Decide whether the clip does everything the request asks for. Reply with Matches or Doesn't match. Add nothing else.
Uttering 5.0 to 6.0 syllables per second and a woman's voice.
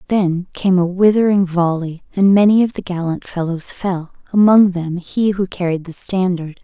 Doesn't match